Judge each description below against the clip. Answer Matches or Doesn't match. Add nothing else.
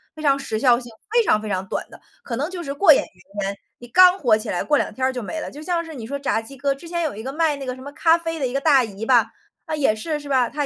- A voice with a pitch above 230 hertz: Matches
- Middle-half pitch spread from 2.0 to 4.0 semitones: Doesn't match